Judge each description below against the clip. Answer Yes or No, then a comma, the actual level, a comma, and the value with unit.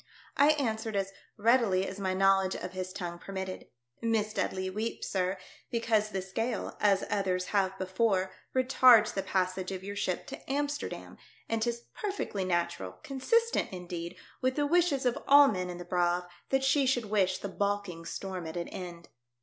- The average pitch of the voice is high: Yes, high, 195 Hz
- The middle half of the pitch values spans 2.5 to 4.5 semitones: Yes, average, 4.2 semitones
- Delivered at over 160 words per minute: Yes, average, 175 wpm